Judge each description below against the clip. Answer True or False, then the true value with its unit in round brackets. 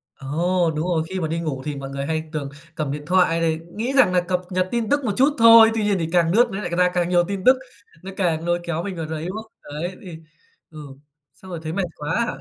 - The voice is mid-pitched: True (175 Hz)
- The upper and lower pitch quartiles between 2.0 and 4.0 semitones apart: True (3.4 semitones)